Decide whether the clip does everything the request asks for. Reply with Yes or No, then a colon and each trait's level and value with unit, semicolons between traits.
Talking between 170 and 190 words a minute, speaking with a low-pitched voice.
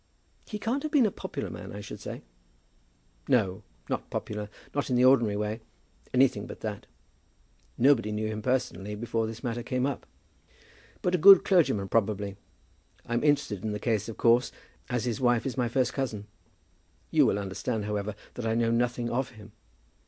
Yes: average, 175 wpm; low, 115 Hz